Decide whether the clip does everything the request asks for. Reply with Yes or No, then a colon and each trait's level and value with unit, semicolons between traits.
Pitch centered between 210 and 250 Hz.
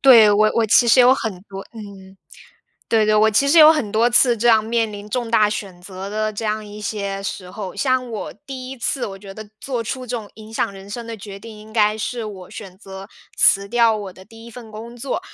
Yes: high, 215 Hz